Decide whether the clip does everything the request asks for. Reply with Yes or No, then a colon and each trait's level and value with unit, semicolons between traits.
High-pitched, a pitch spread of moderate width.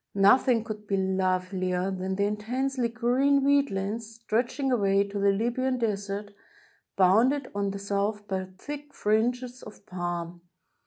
Yes: high, 210 Hz; average, 4.0 semitones